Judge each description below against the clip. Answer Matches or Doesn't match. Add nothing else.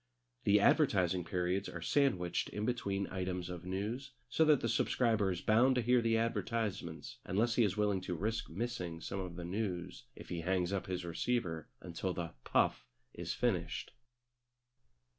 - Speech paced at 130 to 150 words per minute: Doesn't match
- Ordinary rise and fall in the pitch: Matches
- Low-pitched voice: Matches